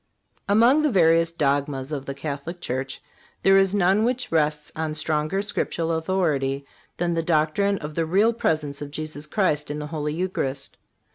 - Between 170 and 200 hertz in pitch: No, medium, 160 Hz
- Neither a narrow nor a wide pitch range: Yes, average, 4.1 semitones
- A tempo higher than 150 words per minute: Yes, average, 165 wpm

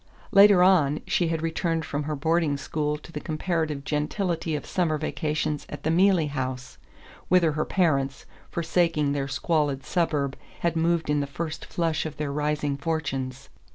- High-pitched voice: No, medium, 155 Hz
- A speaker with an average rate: Yes, average, 160 wpm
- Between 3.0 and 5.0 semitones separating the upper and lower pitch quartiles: No, narrow, 2.6 semitones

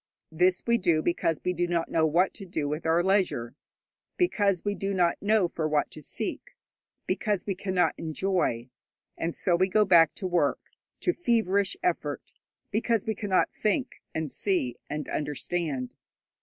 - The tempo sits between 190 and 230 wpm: No, average, 165 wpm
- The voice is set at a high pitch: No, medium, 180 Hz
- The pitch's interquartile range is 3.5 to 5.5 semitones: Yes, average, 4.0 semitones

